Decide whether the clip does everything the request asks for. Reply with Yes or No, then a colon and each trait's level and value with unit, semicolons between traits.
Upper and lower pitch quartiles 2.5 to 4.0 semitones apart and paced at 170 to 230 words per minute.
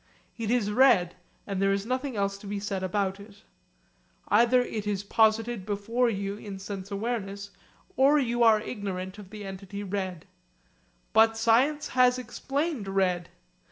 No: average, 3.3 semitones; average, 155 wpm